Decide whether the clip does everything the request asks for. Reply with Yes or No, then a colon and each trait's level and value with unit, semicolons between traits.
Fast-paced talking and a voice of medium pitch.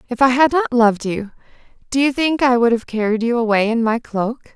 No: fast, 235 wpm; high, 240 Hz